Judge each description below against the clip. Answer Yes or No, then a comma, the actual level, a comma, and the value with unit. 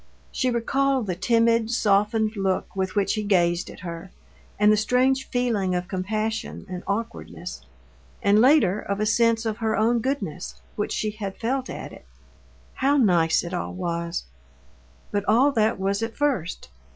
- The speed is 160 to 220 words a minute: Yes, average, 165 wpm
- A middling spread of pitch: Yes, average, 3.6 semitones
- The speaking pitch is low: No, high, 215 Hz